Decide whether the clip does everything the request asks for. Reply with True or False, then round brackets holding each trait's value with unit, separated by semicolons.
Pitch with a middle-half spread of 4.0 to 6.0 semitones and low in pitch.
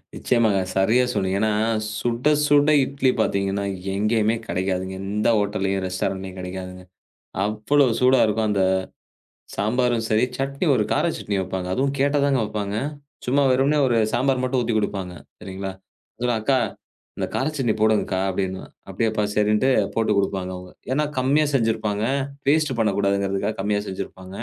True (4.7 semitones; 105 Hz)